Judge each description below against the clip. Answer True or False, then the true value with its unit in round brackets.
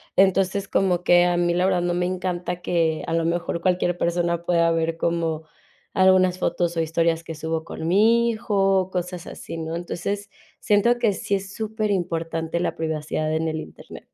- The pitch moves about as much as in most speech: False (2.3 semitones)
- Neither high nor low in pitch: True (175 Hz)